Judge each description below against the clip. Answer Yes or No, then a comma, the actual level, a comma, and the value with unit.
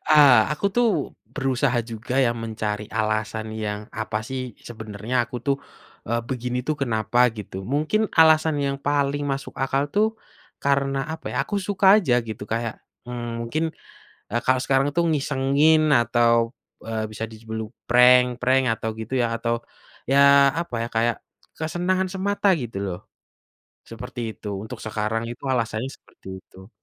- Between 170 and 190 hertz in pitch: No, low, 125 Hz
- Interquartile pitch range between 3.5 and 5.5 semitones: Yes, average, 4.2 semitones